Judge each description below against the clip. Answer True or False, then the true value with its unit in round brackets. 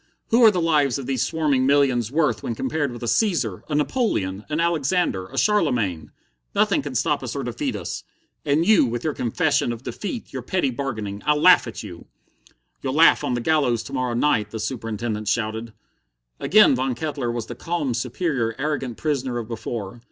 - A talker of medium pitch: False (130 Hz)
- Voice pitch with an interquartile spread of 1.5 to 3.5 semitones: False (5.1 semitones)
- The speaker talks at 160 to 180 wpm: False (190 wpm)